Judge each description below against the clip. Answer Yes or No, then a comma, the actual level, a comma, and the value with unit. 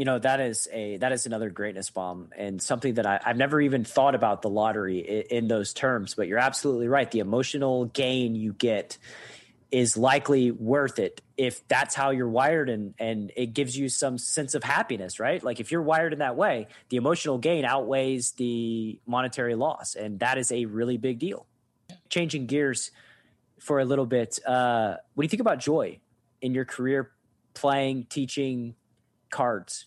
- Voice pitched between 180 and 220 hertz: No, low, 125 Hz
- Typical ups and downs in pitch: Yes, average, 3.2 semitones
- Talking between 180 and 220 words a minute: Yes, average, 185 wpm